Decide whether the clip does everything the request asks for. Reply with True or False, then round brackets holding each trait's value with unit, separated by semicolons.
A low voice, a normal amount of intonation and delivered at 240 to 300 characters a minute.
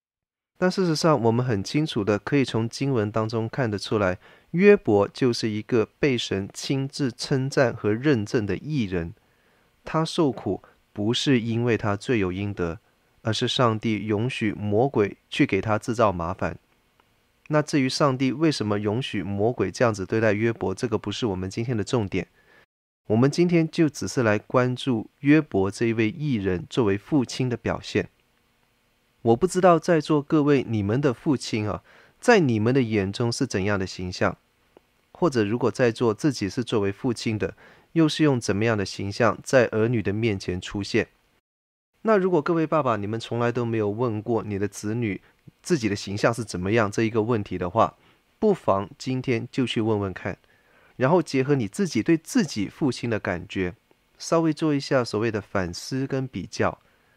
True (115 Hz; 4.9 semitones; 260 characters per minute)